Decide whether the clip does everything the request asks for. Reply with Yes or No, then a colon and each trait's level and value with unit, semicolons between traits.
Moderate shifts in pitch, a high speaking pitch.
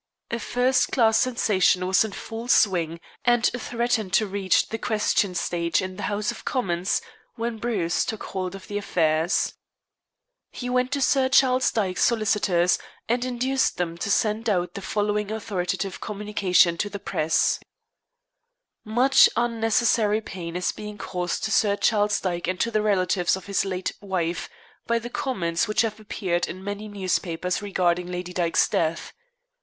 Yes: average, 3.8 semitones; high, 205 Hz